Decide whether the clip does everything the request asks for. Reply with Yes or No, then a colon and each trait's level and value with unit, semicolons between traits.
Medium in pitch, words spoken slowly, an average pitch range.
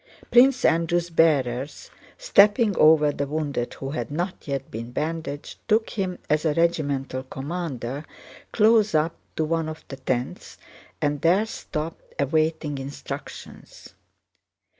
Yes: medium, 155 Hz; slow, 125 wpm; average, 3.6 semitones